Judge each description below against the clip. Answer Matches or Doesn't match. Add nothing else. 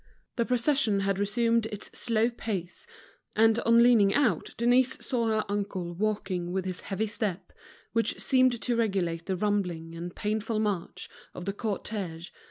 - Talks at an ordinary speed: Matches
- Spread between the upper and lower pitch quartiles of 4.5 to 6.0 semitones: Doesn't match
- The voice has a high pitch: Matches